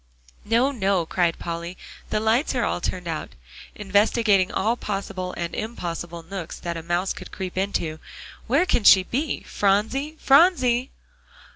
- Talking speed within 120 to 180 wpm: Yes, average, 145 wpm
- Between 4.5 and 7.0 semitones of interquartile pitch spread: Yes, average, 5.3 semitones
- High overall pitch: Yes, high, 195 Hz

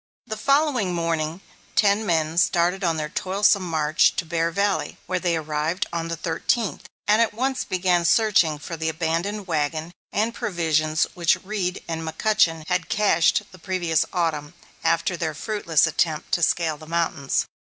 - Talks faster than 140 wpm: Yes, average, 160 wpm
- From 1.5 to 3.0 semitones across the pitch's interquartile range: No, average, 3.4 semitones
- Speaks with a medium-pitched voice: Yes, medium, 170 Hz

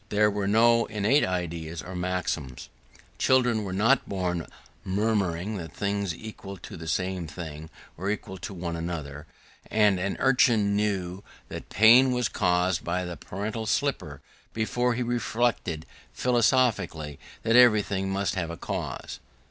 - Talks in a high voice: No, low, 100 Hz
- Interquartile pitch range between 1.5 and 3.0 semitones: No, average, 4.0 semitones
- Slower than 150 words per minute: Yes, average, 140 wpm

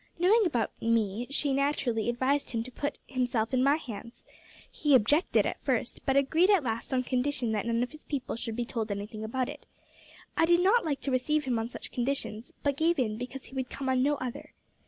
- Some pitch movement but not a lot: Yes, average, 3.7 semitones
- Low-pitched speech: No, very high, 260 Hz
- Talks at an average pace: No, fast, 220 wpm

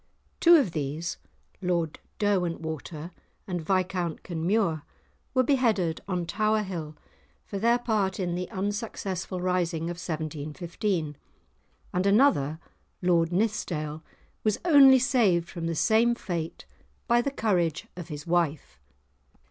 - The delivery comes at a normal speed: No, slow, 120 wpm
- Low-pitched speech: No, medium, 180 Hz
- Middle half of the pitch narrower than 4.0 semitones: No, average, 4.4 semitones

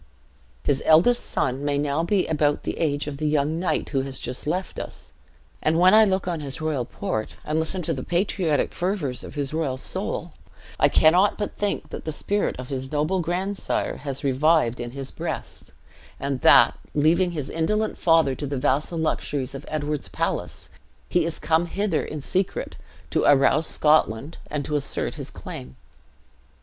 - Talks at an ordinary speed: Yes, average, 180 wpm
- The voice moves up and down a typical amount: Yes, average, 3.6 semitones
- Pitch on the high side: No, medium, 155 Hz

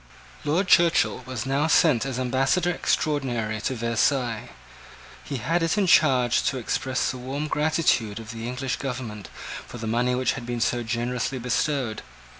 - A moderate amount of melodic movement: Yes, average, 3.7 semitones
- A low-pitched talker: Yes, low, 125 Hz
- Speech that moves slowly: No, average, 160 wpm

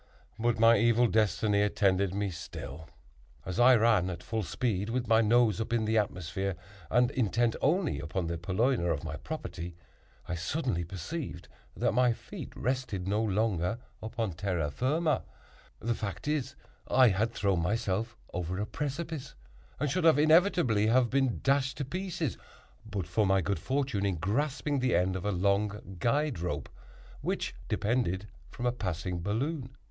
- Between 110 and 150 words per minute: No, average, 160 wpm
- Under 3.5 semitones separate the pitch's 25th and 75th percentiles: No, average, 5.3 semitones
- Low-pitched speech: Yes, low, 110 Hz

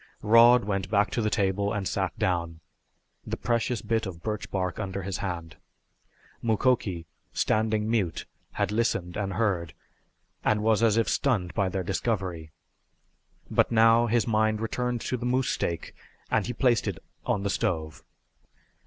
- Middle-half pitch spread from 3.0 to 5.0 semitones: Yes, average, 3.5 semitones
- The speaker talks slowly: No, average, 155 wpm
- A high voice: No, low, 105 Hz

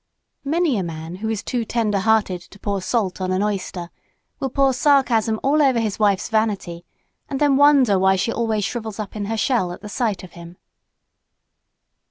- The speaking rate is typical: Yes, average, 190 wpm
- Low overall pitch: No, high, 215 Hz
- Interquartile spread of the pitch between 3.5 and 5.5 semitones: Yes, average, 4.3 semitones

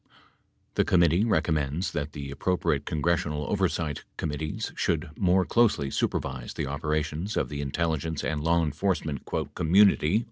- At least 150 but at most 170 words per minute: No, slow, 135 wpm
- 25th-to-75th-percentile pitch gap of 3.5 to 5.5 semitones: No, average, 3.1 semitones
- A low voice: Yes, very low, 80 Hz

